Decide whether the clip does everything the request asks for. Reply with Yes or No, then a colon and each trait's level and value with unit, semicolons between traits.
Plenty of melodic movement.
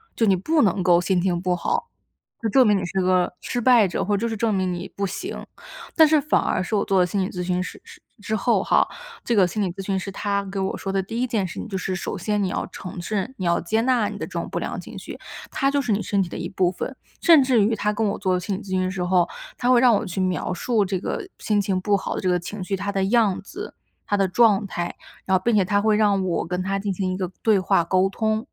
No: average, 2.9 semitones